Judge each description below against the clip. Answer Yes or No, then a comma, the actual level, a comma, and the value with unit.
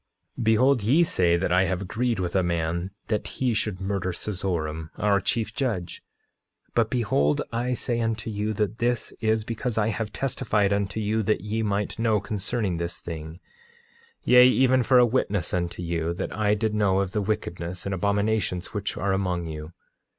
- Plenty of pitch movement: No, average, 3.7 semitones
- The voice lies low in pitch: Yes, low, 105 Hz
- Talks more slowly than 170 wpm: No, average, 180 wpm